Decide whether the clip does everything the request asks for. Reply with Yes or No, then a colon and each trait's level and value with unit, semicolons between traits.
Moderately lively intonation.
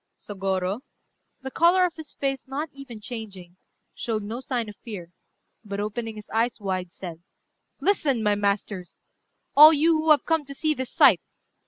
No: wide, 5.9 semitones